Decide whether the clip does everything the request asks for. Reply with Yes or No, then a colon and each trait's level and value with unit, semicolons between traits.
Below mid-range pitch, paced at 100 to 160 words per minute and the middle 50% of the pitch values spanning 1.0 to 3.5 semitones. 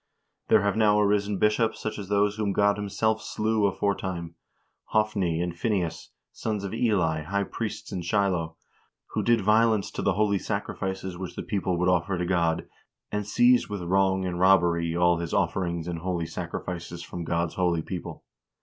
No: very low, 95 Hz; average, 170 wpm; average, 3.2 semitones